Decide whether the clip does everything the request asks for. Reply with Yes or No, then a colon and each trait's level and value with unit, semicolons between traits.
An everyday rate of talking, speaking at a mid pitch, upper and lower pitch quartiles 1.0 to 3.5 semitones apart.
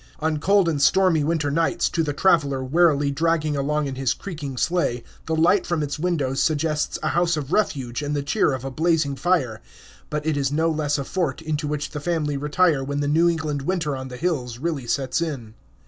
No: fast, 210 wpm; medium, 150 Hz; average, 3.0 semitones